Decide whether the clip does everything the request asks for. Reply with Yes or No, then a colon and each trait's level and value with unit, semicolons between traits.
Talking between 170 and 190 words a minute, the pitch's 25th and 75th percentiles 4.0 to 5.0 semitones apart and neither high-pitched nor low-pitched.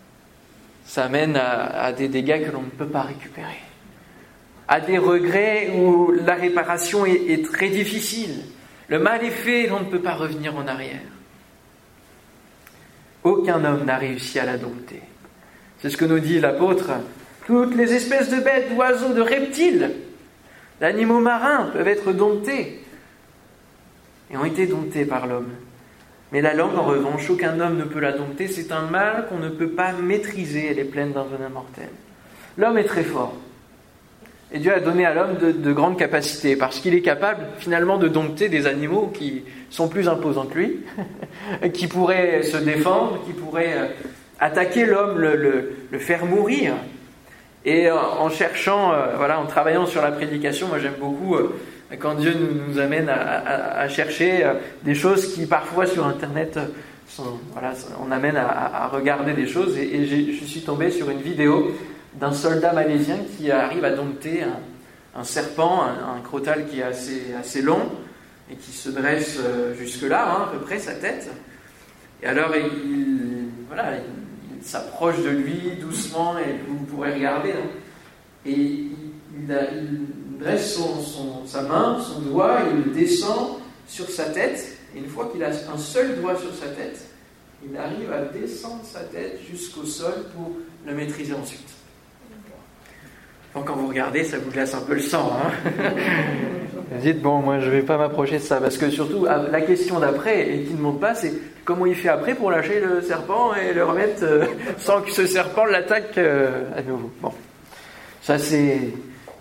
Yes: average, 175 wpm; average, 4.6 semitones; medium, 155 Hz